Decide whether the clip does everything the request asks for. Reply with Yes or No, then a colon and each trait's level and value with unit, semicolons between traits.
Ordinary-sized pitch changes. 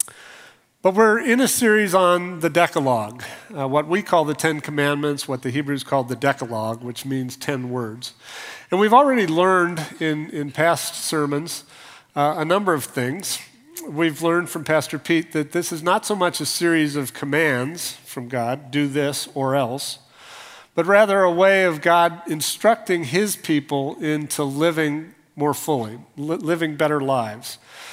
Yes: average, 3.6 semitones